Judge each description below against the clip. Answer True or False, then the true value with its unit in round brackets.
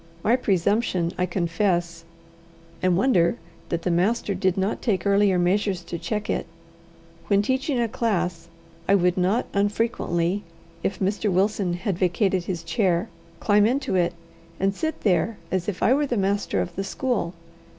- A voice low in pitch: False (195 Hz)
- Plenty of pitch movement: False (3.2 semitones)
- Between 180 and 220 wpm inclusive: False (160 wpm)